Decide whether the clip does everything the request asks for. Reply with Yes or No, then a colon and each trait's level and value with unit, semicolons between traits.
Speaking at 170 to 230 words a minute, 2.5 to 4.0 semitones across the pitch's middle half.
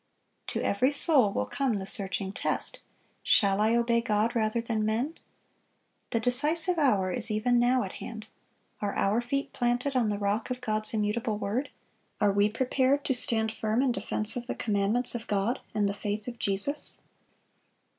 Yes: average, 175 wpm; average, 3.1 semitones